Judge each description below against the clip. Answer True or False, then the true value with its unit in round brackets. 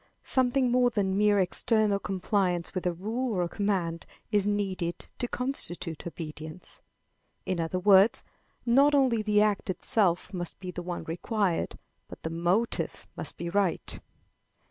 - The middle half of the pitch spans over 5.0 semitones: False (3.9 semitones)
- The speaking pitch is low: False (195 Hz)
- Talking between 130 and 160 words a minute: True (145 wpm)